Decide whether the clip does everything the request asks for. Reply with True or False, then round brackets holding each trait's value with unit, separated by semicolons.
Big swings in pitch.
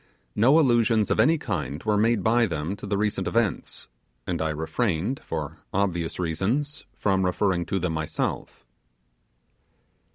True (5.8 semitones)